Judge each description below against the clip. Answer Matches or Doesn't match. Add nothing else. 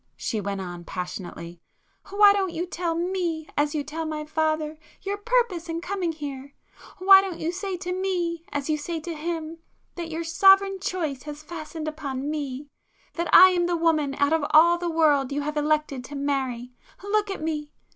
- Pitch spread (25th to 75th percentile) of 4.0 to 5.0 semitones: Doesn't match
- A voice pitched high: Matches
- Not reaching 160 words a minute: Doesn't match